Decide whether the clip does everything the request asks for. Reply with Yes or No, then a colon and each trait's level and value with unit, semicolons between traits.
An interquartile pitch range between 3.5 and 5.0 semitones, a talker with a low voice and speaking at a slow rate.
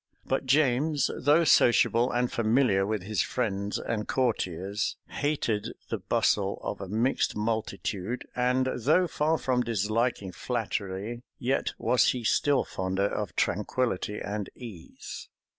Yes: average, 4.0 semitones; low, 115 Hz; slow, 125 wpm